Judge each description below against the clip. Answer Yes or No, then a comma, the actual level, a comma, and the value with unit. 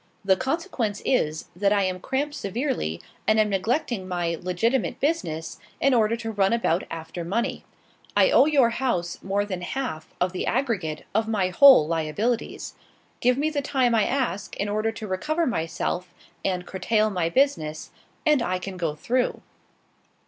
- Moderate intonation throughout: No, wide, 5.8 semitones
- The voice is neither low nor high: No, high, 210 Hz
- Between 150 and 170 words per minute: Yes, average, 165 wpm